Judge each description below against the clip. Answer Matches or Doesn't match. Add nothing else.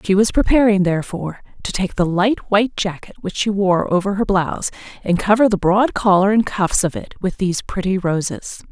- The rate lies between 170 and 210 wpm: Matches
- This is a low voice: Doesn't match